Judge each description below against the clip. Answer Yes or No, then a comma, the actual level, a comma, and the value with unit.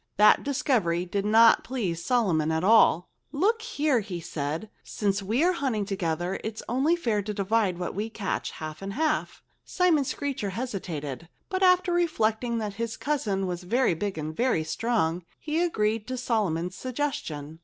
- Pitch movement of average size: No, wide, 6.4 semitones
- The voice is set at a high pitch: Yes, high, 215 Hz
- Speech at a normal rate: Yes, average, 165 wpm